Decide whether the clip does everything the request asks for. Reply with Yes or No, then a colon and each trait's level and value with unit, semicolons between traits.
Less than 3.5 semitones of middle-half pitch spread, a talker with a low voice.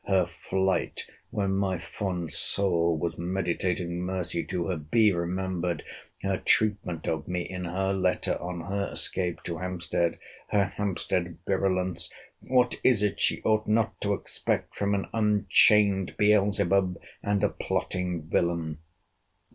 Yes: narrow, 2.5 semitones; very low, 95 Hz